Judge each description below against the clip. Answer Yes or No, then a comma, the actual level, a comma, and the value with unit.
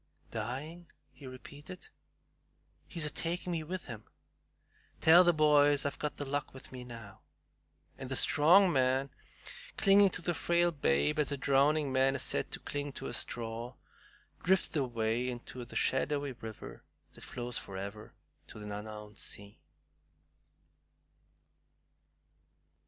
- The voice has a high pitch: No, low, 135 Hz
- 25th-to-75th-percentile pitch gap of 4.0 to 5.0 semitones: Yes, average, 4.4 semitones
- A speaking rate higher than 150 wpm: No, slow, 135 wpm